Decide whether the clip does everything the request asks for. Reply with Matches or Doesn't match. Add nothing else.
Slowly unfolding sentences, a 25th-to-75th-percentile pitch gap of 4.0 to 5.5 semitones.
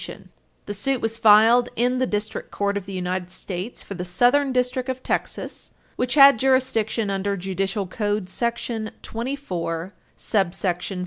Doesn't match